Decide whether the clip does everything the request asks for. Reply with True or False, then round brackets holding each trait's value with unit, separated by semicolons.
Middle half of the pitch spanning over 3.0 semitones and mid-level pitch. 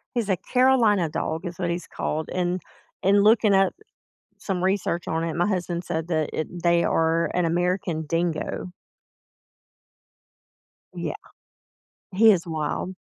False (2.6 semitones; 175 Hz)